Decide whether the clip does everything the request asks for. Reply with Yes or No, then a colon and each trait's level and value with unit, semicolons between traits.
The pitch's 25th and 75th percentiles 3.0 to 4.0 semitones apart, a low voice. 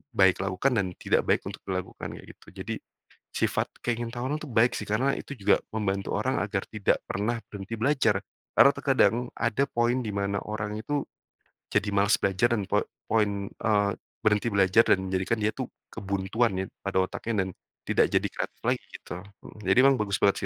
Yes: average, 3.3 semitones; low, 105 Hz